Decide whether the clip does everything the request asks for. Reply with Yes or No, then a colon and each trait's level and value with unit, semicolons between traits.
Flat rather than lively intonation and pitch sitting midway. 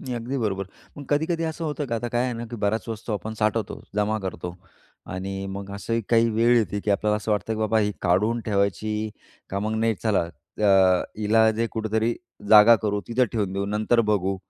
No: narrow, 2.1 semitones; low, 110 Hz